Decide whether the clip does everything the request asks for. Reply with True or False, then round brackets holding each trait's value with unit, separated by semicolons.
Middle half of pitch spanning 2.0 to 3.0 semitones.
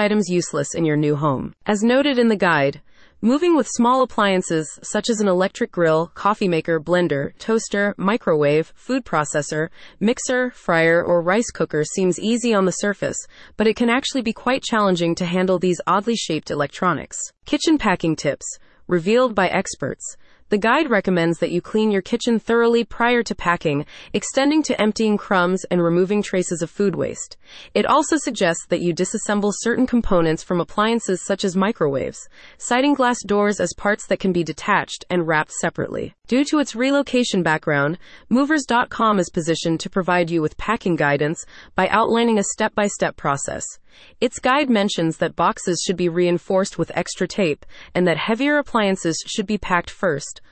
False (5.2 semitones)